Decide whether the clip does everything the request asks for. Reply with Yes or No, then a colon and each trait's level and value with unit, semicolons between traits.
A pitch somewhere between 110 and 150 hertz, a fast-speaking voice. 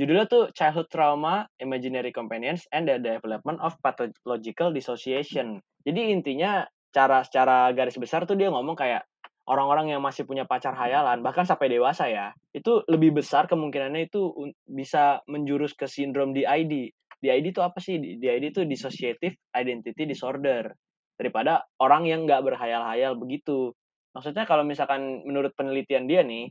Yes: medium, 140 Hz; fast, 145 wpm